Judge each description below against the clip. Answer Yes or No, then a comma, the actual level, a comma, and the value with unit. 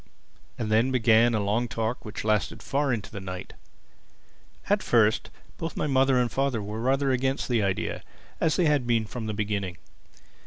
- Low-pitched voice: Yes, low, 115 Hz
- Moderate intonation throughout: Yes, average, 3.7 semitones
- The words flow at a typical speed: Yes, average, 170 wpm